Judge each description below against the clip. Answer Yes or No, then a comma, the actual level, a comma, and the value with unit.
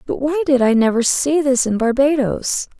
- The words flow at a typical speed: Yes, average, 195 wpm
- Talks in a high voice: Yes, very high, 265 Hz